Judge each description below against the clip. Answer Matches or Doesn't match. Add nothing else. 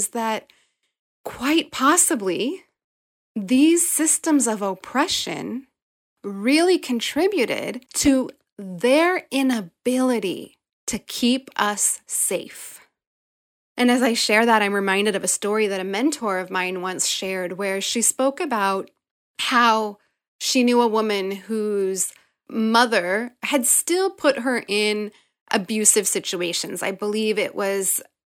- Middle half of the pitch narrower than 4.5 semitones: Doesn't match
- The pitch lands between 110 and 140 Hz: Doesn't match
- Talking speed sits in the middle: Doesn't match